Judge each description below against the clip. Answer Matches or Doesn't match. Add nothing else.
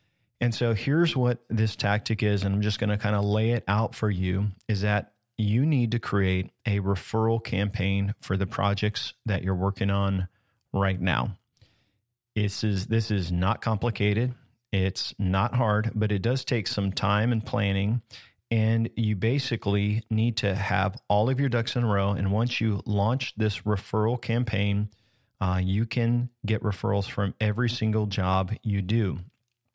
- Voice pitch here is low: Matches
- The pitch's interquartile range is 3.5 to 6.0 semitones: Doesn't match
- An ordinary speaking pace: Matches